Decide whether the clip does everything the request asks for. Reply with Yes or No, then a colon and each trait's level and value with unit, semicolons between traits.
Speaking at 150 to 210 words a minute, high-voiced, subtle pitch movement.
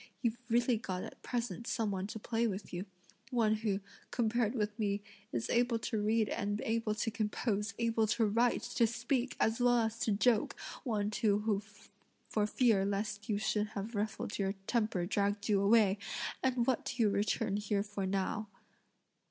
Yes: average, 175 wpm; high, 215 Hz; narrow, 2.3 semitones